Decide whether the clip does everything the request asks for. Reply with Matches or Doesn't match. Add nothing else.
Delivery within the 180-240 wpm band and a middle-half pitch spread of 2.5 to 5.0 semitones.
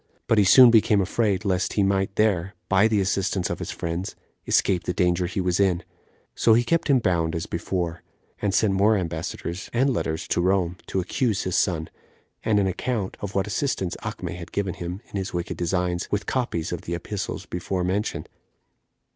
Matches